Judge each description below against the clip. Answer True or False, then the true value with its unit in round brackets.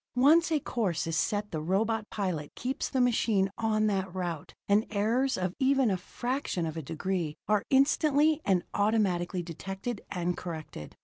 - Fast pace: False (165 wpm)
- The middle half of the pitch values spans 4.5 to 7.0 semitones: True (5.6 semitones)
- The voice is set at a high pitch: True (200 Hz)